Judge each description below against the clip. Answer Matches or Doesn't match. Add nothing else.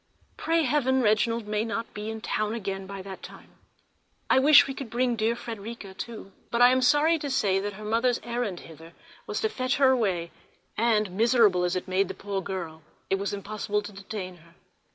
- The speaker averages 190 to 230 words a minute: Matches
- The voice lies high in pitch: Matches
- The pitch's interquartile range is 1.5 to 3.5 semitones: Doesn't match